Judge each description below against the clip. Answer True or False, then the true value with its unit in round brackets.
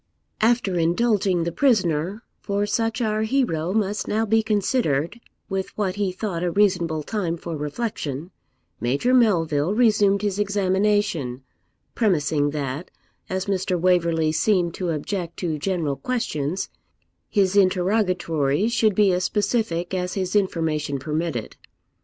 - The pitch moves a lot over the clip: False (4.3 semitones)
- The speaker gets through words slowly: True (130 wpm)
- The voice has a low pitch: False (185 Hz)